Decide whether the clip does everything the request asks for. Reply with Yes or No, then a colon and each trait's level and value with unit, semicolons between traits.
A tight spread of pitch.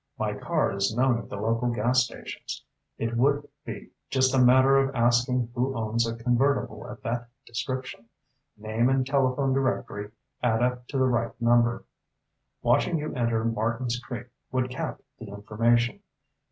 Yes: narrow, 2.1 semitones